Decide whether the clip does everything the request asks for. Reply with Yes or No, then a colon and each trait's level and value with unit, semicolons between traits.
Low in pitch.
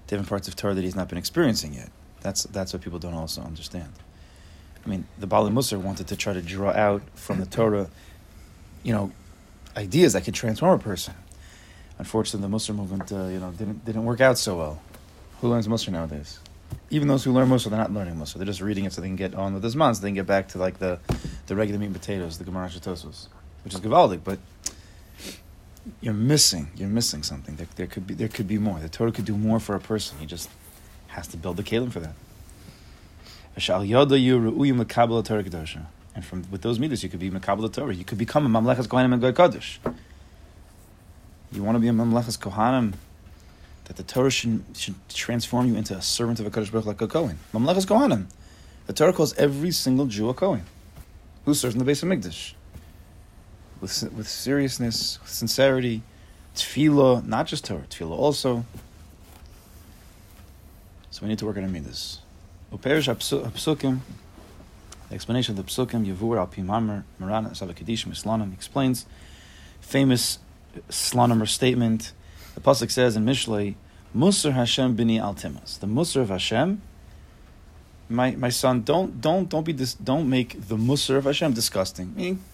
Yes: low, 100 Hz